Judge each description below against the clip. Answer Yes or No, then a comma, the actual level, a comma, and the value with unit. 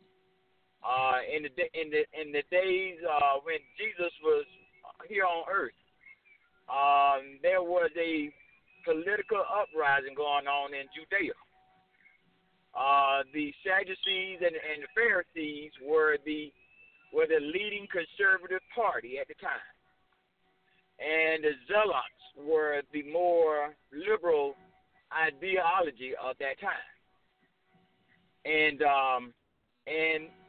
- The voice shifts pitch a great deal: No, average, 4.4 semitones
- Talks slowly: Yes, slow, 110 wpm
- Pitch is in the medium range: Yes, medium, 160 Hz